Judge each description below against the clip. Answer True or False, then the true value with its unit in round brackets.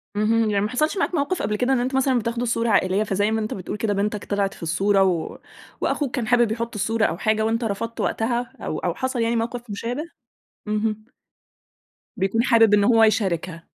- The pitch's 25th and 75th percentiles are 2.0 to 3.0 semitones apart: True (2.7 semitones)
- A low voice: False (225 Hz)